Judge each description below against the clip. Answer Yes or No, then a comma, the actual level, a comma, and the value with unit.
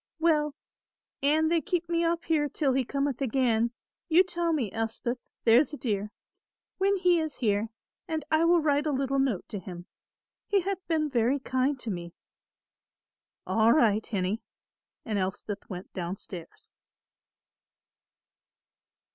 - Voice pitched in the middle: No, very high, 270 Hz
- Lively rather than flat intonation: Yes, wide, 6.4 semitones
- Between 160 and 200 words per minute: No, average, 145 wpm